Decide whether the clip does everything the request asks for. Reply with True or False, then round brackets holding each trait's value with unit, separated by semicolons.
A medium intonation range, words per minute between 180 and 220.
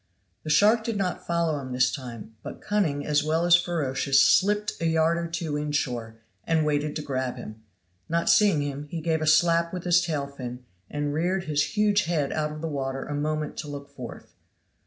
True (3.2 semitones; 200 wpm)